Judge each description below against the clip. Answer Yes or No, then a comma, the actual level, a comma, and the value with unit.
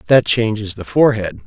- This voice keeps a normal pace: Yes, average, 165 wpm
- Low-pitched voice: Yes, low, 110 Hz